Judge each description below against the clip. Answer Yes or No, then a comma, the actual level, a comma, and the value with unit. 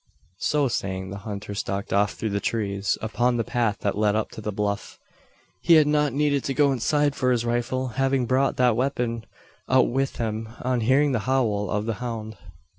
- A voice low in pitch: Yes, low, 120 Hz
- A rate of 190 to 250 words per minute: Yes, average, 195 wpm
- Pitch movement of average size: Yes, average, 4.0 semitones